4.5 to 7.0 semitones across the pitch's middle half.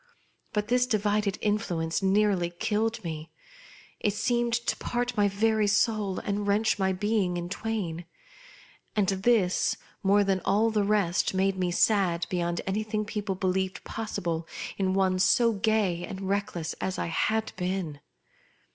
No: average, 2.7 semitones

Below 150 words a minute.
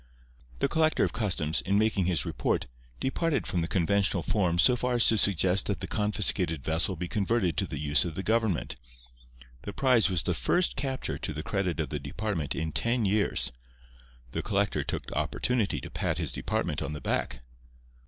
No: average, 185 wpm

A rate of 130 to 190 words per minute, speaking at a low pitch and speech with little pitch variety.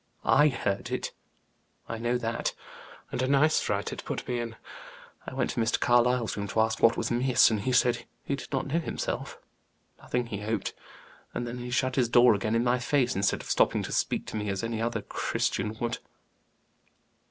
No: average, 200 wpm; low, 120 Hz; narrow, 2.0 semitones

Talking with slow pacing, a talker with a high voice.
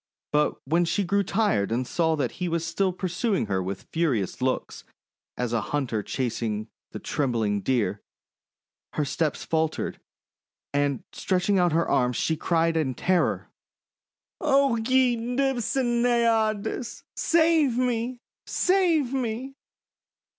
No: slow, 130 wpm; medium, 175 Hz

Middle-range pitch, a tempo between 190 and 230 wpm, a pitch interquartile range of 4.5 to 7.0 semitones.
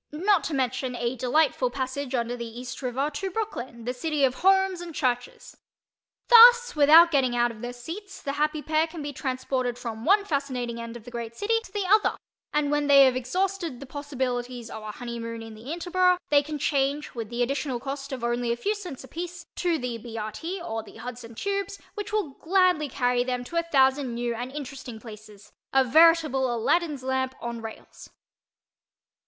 No: very high, 265 Hz; average, 195 wpm; average, 5.3 semitones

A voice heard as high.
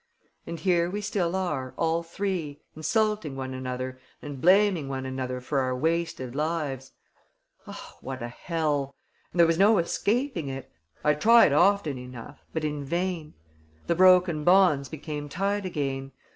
No: medium, 155 Hz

